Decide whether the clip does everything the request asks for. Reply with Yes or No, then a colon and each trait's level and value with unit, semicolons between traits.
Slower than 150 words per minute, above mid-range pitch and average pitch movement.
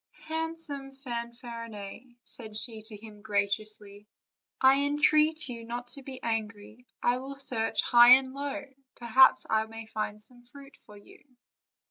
Yes: average, 140 wpm; high, 240 Hz; average, 3.8 semitones